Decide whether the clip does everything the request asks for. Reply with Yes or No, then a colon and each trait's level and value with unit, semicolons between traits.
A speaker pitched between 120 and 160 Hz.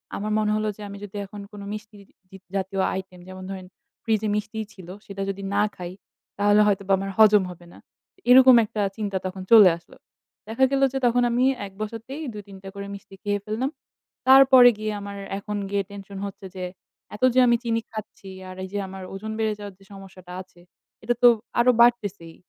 No: high, 205 Hz